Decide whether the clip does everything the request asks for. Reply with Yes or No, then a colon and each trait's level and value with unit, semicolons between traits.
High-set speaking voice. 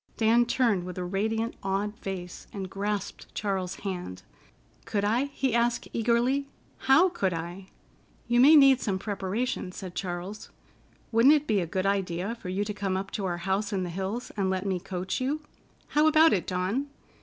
Yes: high, 200 Hz